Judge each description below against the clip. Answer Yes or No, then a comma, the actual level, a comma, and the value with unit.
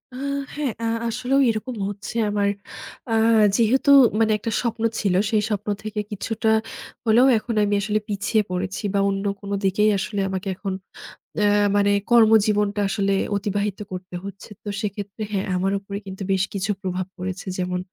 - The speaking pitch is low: No, high, 205 Hz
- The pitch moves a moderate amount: No, narrow, 2.0 semitones